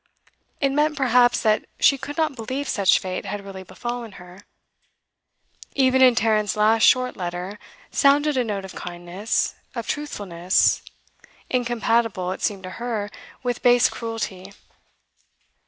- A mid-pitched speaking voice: No, high, 225 Hz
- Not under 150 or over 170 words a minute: No, slow, 135 wpm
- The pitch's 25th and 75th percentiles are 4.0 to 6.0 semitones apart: Yes, average, 4.8 semitones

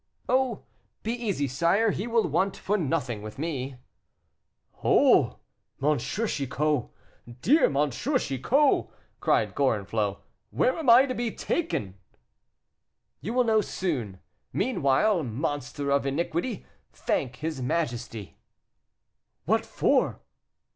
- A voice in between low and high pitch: Yes, medium, 160 Hz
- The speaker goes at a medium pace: No, slow, 115 wpm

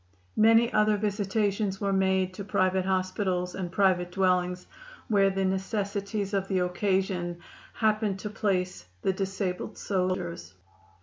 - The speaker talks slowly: Yes, slow, 125 wpm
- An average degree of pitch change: No, narrow, 1.7 semitones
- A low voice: No, high, 190 Hz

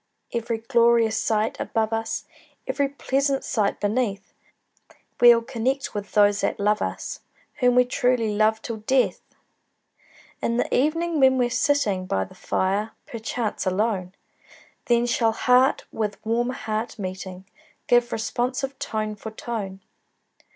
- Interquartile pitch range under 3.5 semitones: Yes, average, 2.9 semitones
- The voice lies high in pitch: Yes, high, 230 Hz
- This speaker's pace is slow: Yes, slow, 130 wpm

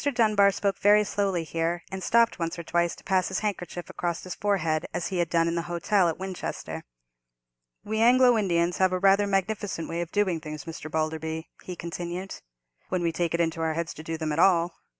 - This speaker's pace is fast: Yes, fast, 210 wpm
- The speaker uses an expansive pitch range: No, average, 2.9 semitones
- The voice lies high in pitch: No, medium, 175 Hz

